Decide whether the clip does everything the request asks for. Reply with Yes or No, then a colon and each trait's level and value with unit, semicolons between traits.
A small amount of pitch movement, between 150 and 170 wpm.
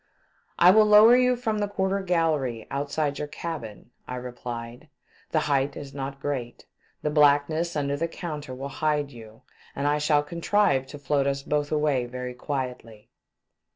No: average, 3.7 semitones; average, 165 wpm